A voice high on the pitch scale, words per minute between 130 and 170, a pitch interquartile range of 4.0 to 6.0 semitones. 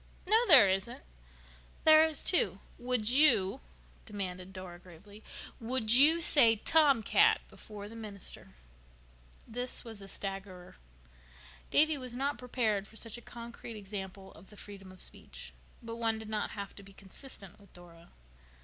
Yes: high, 220 Hz; average, 150 wpm; average, 4.4 semitones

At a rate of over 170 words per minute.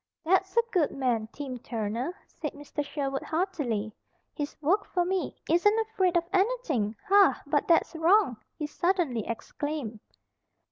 No: average, 140 wpm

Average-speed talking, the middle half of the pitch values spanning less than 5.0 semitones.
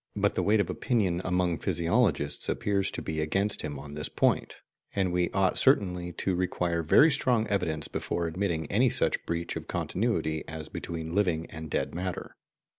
Yes: average, 180 wpm; average, 3.7 semitones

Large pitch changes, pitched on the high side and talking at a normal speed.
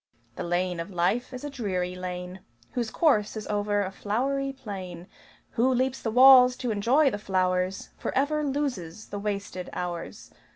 Yes: wide, 5.9 semitones; high, 205 Hz; average, 160 wpm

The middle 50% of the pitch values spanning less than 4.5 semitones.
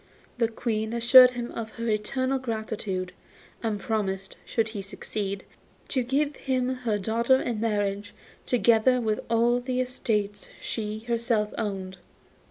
Yes: average, 2.8 semitones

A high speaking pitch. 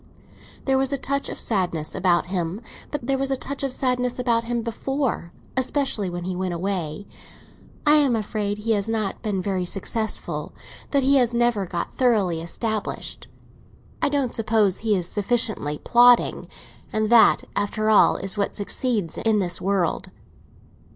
Yes: high, 215 Hz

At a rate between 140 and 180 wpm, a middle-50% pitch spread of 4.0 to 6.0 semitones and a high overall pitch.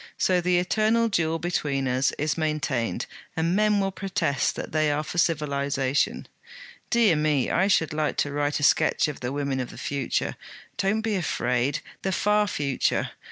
No: average, 170 wpm; average, 5.2 semitones; medium, 155 Hz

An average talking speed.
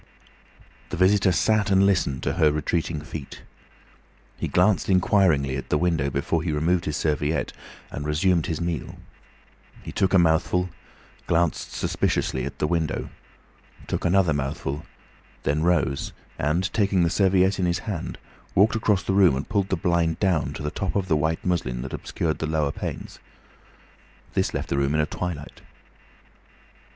Yes: average, 160 wpm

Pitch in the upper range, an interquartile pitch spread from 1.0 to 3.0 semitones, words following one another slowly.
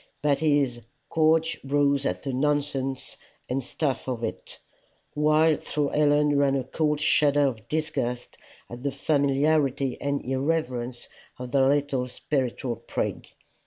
No: medium, 140 Hz; narrow, 2.5 semitones; slow, 130 wpm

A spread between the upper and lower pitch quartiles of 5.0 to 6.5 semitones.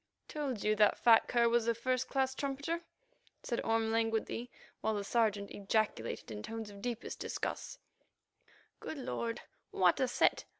No: average, 2.9 semitones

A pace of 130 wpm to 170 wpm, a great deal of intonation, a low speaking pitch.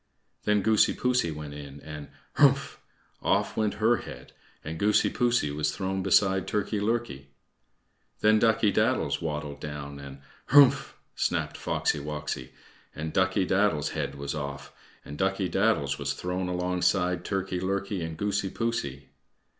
Yes: average, 140 wpm; wide, 5.8 semitones; very low, 90 Hz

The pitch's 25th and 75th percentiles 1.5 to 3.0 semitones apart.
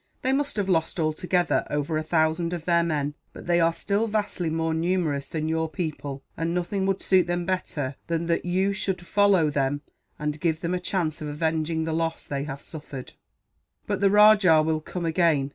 Yes: average, 2.7 semitones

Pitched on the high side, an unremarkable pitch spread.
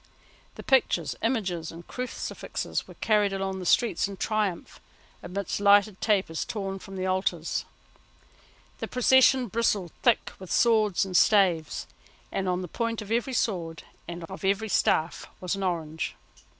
Yes: high, 195 Hz; average, 3.4 semitones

